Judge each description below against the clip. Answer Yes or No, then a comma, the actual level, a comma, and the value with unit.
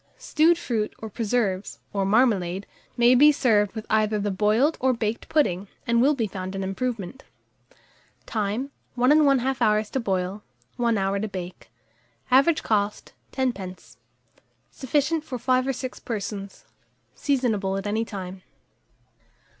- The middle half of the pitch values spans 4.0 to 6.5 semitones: Yes, average, 4.4 semitones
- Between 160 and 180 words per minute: No, average, 140 wpm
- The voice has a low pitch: No, high, 220 Hz